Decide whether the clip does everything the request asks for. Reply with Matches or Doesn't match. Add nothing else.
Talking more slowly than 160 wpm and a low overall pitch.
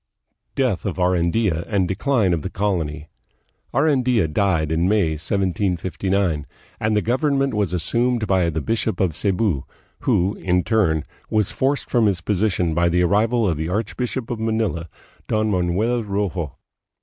Matches